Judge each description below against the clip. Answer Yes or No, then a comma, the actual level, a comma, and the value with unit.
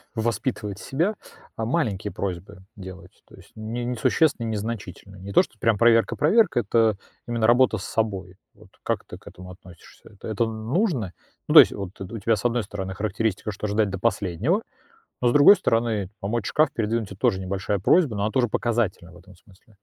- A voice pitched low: Yes, low, 110 Hz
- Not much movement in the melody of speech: No, average, 3.4 semitones